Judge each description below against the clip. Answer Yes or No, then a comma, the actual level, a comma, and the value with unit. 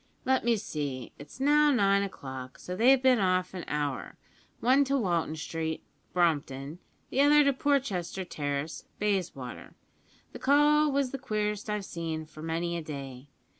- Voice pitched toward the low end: No, medium, 185 Hz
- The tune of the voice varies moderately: No, wide, 8.9 semitones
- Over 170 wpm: No, average, 155 wpm